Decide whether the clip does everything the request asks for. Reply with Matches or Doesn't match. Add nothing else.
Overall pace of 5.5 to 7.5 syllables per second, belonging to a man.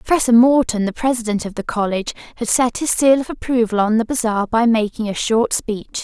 Doesn't match